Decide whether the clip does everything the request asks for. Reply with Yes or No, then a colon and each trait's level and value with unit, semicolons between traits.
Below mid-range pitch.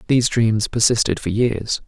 Yes: low, 110 Hz